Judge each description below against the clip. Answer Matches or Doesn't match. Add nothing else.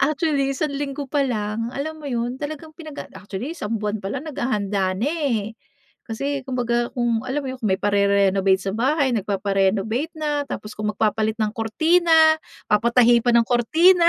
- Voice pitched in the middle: Doesn't match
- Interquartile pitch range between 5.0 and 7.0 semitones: Matches